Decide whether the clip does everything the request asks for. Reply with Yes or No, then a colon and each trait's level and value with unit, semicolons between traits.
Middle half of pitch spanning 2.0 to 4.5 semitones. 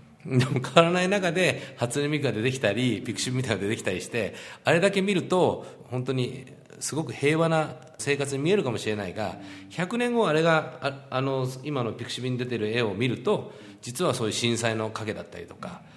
No: average, 5.2 semitones